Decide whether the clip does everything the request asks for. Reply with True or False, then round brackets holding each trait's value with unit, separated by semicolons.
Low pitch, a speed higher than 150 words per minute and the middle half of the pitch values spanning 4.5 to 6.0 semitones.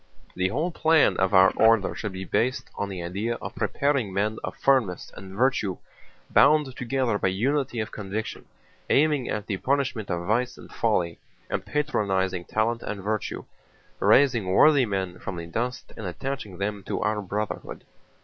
True (110 Hz; 160 wpm; 5.3 semitones)